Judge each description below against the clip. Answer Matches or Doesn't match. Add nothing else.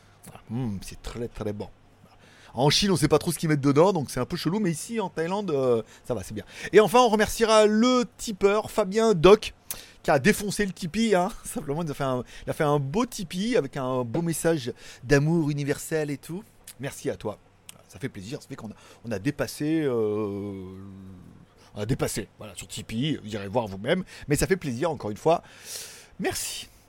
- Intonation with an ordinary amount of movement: Doesn't match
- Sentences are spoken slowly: Doesn't match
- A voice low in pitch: Doesn't match